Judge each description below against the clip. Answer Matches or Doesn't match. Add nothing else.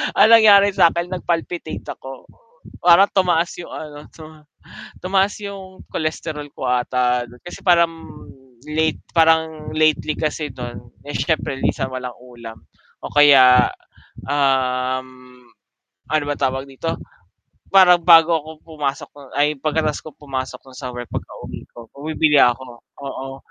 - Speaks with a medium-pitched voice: Matches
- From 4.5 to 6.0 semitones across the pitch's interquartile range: Doesn't match